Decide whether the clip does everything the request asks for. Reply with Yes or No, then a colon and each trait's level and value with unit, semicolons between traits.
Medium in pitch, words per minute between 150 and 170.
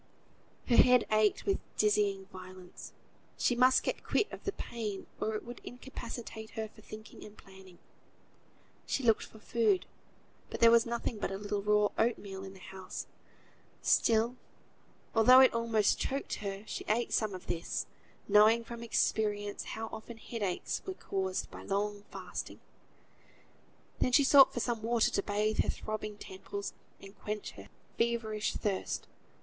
No: high, 215 Hz; average, 155 wpm